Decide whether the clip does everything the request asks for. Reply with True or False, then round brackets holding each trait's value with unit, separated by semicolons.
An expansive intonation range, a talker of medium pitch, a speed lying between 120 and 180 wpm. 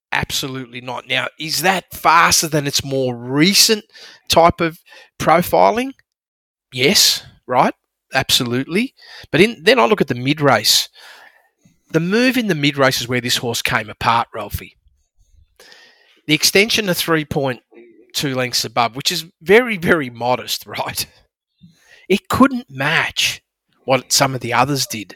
True (6.9 semitones; 150 Hz; 140 wpm)